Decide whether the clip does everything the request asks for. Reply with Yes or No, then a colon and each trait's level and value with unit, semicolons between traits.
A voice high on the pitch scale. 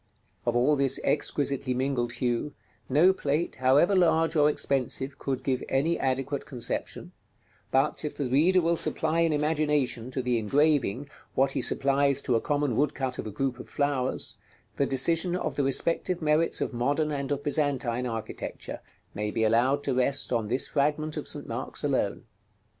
No: medium, 140 Hz